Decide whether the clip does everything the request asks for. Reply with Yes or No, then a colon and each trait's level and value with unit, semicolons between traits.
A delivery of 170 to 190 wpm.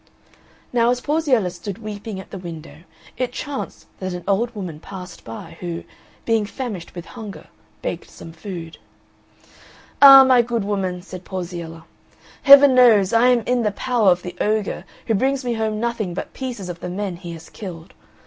Yes: average, 175 wpm